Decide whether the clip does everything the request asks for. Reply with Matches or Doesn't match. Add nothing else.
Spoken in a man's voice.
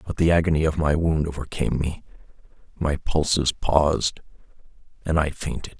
Matches